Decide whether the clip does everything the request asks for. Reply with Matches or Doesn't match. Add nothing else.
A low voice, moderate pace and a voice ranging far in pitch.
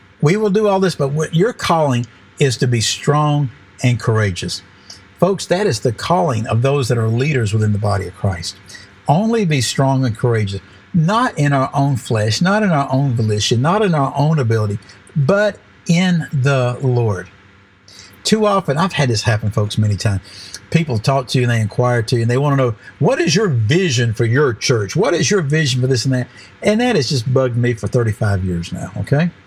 Doesn't match